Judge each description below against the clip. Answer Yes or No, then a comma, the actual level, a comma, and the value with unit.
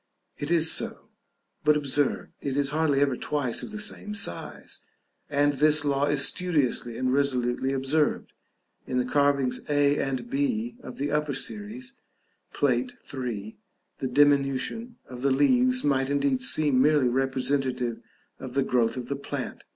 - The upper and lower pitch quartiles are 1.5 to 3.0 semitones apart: Yes, narrow, 2.5 semitones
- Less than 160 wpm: Yes, average, 150 wpm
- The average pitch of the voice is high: No, medium, 140 Hz